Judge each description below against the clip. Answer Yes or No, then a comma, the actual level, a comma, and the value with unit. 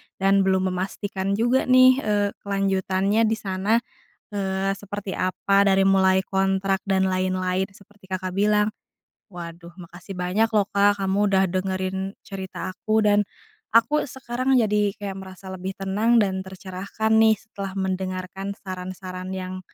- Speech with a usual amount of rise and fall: No, narrow, 1.6 semitones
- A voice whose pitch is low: No, high, 195 Hz